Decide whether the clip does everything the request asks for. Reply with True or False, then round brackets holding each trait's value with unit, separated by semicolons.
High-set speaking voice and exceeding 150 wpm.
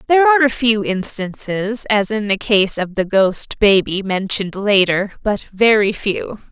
True (210 Hz; 165 wpm)